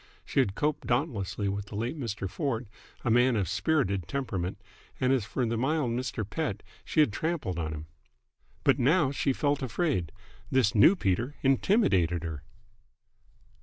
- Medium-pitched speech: No, low, 120 Hz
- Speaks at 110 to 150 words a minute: No, average, 165 wpm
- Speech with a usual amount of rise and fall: No, wide, 5.9 semitones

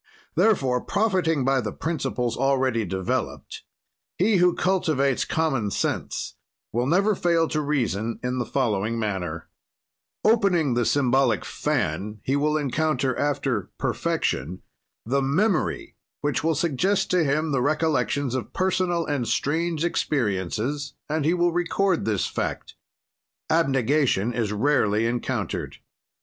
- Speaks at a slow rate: Yes, slow, 125 wpm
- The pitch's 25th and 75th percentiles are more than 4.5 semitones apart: Yes, wide, 5.5 semitones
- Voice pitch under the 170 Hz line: Yes, medium, 140 Hz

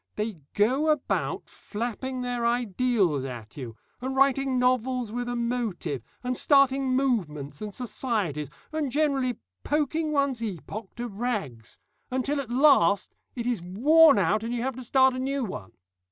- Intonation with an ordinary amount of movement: Yes, average, 4.4 semitones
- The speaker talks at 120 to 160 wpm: Yes, average, 155 wpm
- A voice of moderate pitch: No, high, 245 Hz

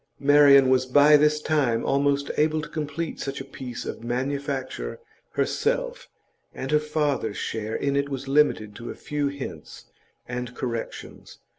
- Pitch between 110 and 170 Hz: Yes, medium, 140 Hz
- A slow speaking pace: No, average, 150 wpm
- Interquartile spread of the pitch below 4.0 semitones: Yes, narrow, 2.6 semitones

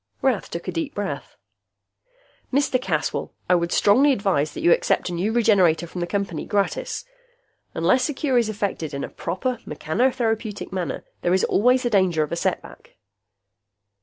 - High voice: Yes, high, 200 Hz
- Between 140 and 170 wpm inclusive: Yes, average, 165 wpm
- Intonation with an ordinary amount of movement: No, wide, 5.9 semitones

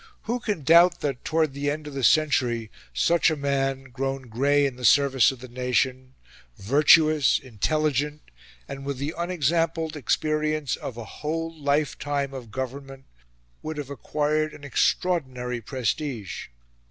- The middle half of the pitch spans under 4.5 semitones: Yes, average, 2.9 semitones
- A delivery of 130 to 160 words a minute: Yes, average, 145 wpm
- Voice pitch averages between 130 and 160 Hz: Yes, medium, 140 Hz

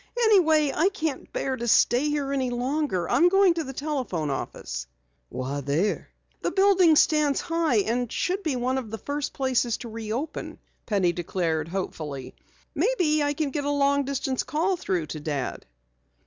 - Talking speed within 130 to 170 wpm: Yes, average, 165 wpm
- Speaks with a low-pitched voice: No, very high, 270 Hz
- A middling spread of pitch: No, wide, 7.0 semitones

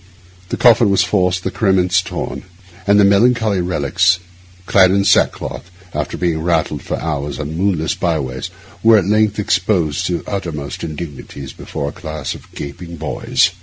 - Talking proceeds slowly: No, average, 155 wpm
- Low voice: Yes, very low, 90 Hz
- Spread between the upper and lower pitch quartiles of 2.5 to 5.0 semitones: Yes, average, 4.3 semitones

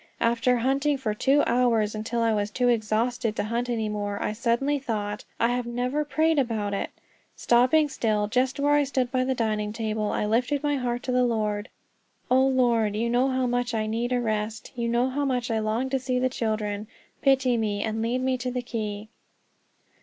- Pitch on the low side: No, high, 240 Hz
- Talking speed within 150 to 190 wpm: No, fast, 205 wpm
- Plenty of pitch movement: No, average, 2.9 semitones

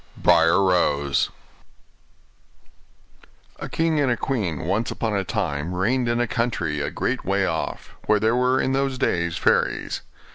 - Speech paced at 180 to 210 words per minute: No, average, 145 wpm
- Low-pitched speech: Yes, low, 105 Hz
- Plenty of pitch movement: Yes, wide, 6.6 semitones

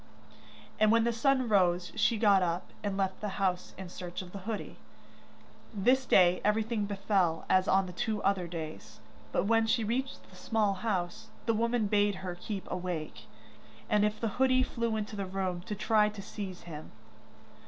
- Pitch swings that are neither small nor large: Yes, average, 3.3 semitones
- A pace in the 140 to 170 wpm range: No, average, 180 wpm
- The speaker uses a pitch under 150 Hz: No, high, 200 Hz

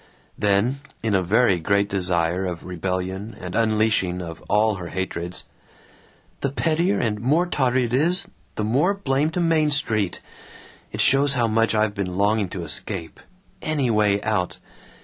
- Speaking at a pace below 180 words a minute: Yes, average, 155 wpm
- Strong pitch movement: Yes, wide, 6.0 semitones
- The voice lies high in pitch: No, low, 105 Hz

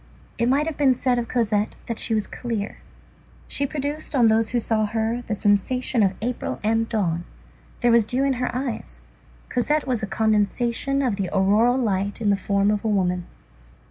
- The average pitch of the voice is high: Yes, high, 225 Hz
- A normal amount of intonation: Yes, average, 3.4 semitones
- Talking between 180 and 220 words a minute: Yes, average, 190 wpm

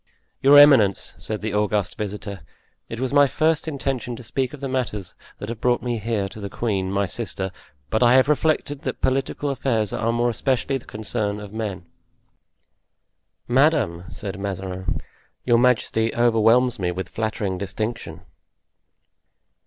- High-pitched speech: No, low, 115 Hz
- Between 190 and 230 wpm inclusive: No, average, 155 wpm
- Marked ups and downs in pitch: No, average, 4.2 semitones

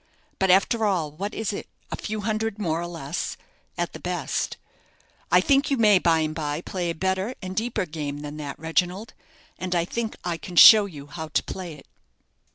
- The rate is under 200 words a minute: No, fast, 205 wpm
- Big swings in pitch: No, average, 4.8 semitones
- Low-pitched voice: No, medium, 180 Hz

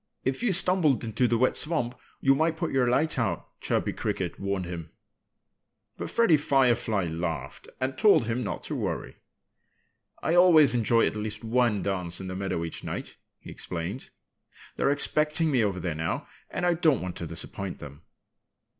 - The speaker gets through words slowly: No, average, 170 wpm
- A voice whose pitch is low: Yes, low, 120 Hz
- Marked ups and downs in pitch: Yes, wide, 8.1 semitones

